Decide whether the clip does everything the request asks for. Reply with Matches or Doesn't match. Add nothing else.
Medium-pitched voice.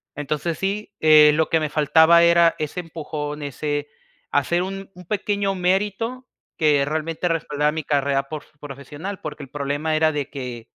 Matches